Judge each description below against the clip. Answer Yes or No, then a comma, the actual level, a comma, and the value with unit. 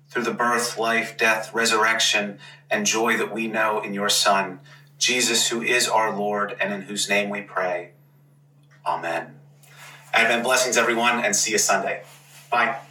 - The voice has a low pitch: Yes, low, 115 Hz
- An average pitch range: Yes, average, 3.0 semitones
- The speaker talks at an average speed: Yes, average, 160 wpm